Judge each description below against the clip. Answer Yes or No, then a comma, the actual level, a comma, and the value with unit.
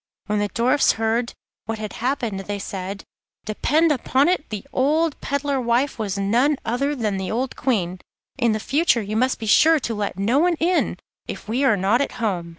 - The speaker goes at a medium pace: Yes, average, 190 wpm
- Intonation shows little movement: No, average, 5.1 semitones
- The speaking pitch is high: Yes, high, 235 Hz